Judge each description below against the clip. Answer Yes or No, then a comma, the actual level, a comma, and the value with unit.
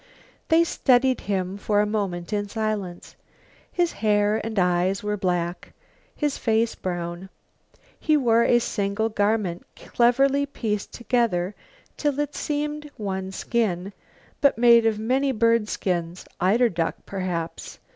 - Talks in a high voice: Yes, high, 215 Hz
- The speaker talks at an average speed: No, slow, 125 wpm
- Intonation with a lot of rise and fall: No, average, 4.3 semitones